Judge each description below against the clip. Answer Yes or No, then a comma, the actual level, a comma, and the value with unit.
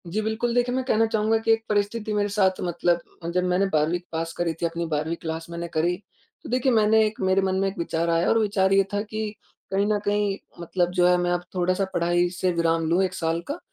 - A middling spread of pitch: Yes, average, 3.7 semitones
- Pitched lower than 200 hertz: Yes, medium, 185 Hz